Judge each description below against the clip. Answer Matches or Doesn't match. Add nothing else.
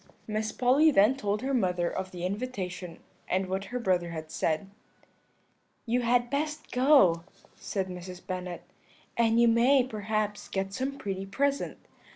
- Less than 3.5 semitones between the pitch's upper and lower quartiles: Doesn't match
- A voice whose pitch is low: Doesn't match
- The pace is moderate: Matches